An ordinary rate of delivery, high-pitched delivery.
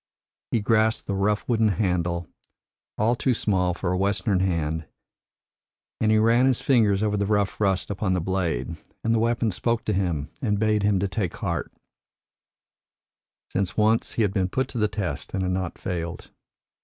No: average, 175 wpm; low, 100 Hz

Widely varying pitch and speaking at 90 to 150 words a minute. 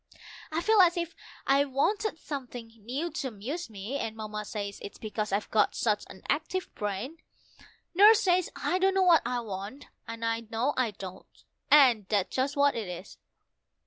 No: wide, 7.3 semitones; average, 175 wpm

